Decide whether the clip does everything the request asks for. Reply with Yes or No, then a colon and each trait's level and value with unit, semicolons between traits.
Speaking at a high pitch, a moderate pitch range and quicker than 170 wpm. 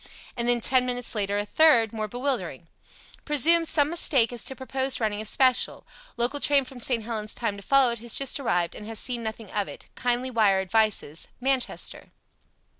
Yes: high, 240 Hz; average, 3.6 semitones; average, 190 wpm